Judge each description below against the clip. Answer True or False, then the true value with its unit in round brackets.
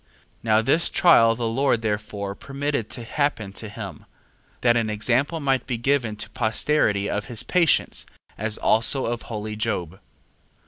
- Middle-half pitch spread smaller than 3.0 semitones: False (4.2 semitones)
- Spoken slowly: False (155 wpm)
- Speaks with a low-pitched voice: True (115 Hz)